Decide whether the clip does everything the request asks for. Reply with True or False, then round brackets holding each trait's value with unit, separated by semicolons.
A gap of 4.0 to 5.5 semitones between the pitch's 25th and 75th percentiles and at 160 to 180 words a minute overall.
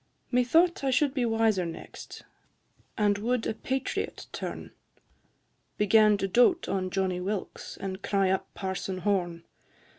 False (4.4 semitones; 140 wpm)